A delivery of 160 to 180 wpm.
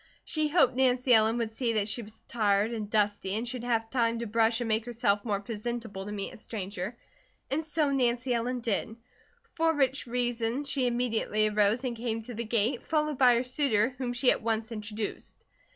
No: average, 200 wpm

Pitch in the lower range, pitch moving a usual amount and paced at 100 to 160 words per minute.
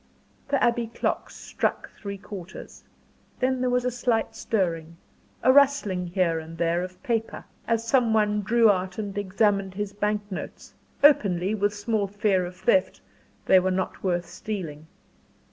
No: high, 205 Hz; average, 3.7 semitones; average, 155 wpm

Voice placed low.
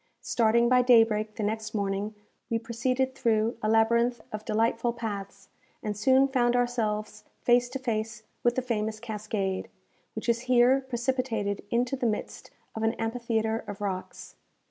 No: high, 230 Hz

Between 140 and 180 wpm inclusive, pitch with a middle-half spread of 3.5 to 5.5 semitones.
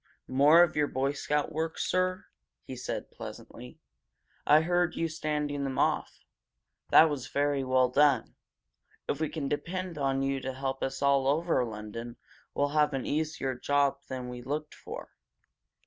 No: average, 160 wpm; average, 2.7 semitones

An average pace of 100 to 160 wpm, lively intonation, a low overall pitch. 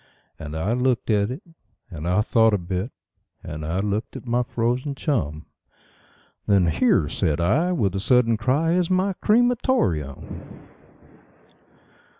Yes: average, 150 wpm; wide, 6.9 semitones; low, 110 Hz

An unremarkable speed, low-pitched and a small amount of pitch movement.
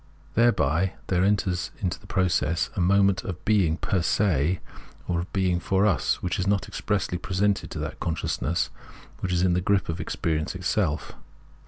Yes: average, 170 wpm; very low, 90 Hz; narrow, 2.2 semitones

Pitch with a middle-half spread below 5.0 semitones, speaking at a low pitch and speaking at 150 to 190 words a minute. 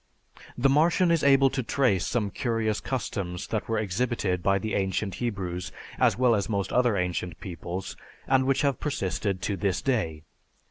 No: wide, 5.5 semitones; low, 110 Hz; average, 170 wpm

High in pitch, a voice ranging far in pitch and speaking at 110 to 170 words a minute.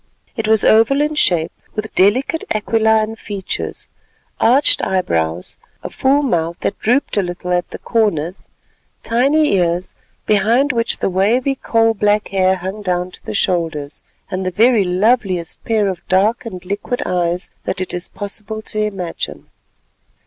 No: high, 205 Hz; average, 4.0 semitones; average, 150 wpm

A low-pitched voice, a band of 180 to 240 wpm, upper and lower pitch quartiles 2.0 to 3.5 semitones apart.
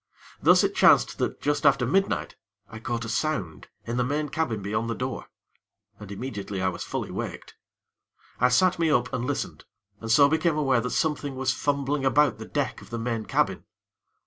No: low, 125 Hz; average, 190 wpm; average, 4.3 semitones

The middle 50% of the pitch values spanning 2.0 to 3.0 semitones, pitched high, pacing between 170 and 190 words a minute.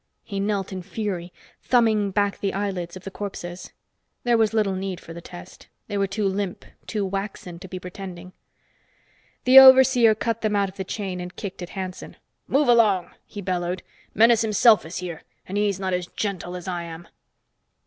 Yes: average, 2.7 semitones; high, 195 Hz; average, 185 wpm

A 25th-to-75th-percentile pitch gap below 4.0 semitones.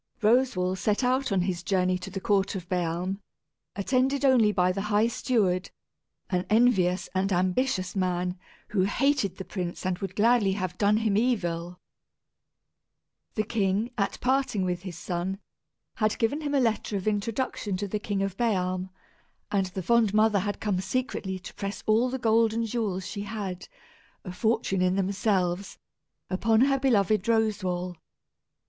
Yes: average, 3.5 semitones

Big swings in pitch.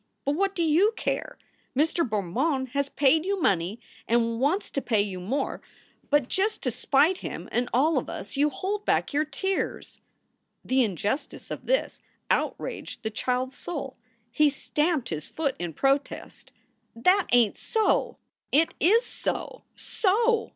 Yes: wide, 6.6 semitones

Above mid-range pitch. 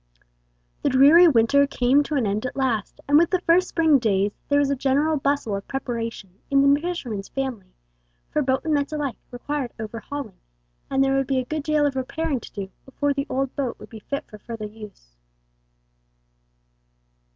Yes: very high, 270 Hz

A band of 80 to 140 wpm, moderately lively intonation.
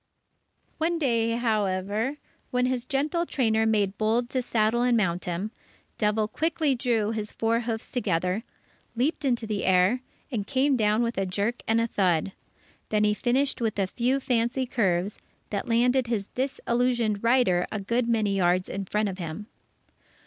No: average, 165 wpm; average, 3.4 semitones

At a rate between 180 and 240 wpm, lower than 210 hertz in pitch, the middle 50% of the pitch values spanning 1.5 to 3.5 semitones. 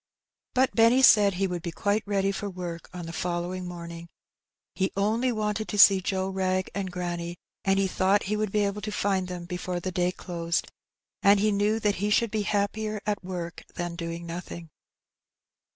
Yes: average, 190 wpm; high, 190 Hz; average, 2.8 semitones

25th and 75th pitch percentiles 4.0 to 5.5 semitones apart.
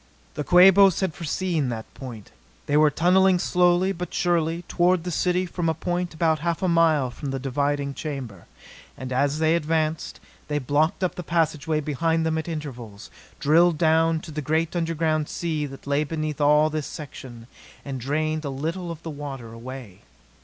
No: average, 3.0 semitones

